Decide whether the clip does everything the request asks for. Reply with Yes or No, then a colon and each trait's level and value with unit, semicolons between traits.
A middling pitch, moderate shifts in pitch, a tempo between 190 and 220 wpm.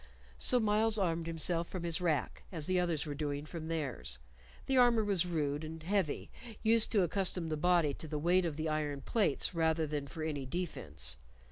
Yes: medium, 165 Hz; average, 3.4 semitones; average, 195 wpm